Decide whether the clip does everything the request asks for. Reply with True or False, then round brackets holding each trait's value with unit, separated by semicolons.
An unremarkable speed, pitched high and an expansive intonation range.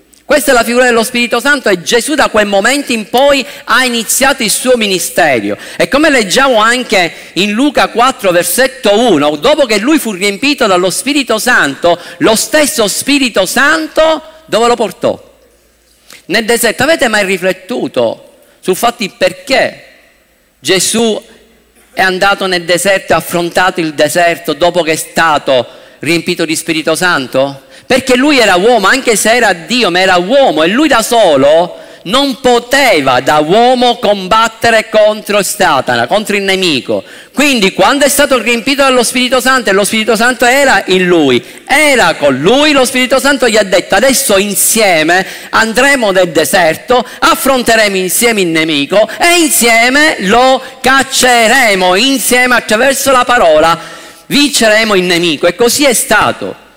True (150 wpm; 230 Hz; 6.1 semitones)